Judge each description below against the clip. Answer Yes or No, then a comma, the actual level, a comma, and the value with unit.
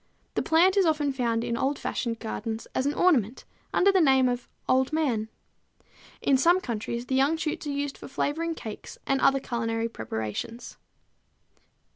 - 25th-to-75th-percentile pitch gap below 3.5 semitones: No, average, 4.7 semitones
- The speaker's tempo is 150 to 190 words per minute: Yes, average, 165 wpm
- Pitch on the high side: Yes, very high, 265 Hz